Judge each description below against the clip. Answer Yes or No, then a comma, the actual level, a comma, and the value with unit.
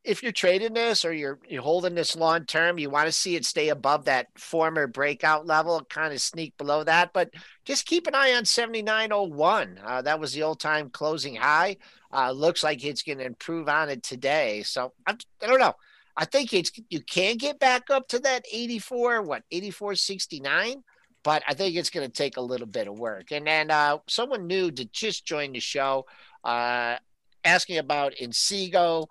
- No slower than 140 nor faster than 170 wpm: No, average, 195 wpm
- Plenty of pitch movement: Yes, wide, 6.5 semitones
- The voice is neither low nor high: Yes, medium, 165 Hz